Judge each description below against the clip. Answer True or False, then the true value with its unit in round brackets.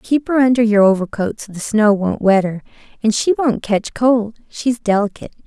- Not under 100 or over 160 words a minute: False (195 wpm)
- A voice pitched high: True (220 Hz)